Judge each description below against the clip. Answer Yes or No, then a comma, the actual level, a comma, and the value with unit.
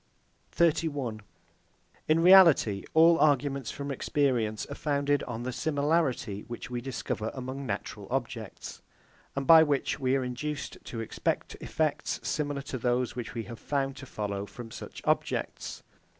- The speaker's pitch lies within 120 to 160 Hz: Yes, low, 135 Hz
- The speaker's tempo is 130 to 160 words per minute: Yes, average, 145 wpm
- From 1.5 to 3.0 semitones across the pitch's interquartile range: No, average, 3.7 semitones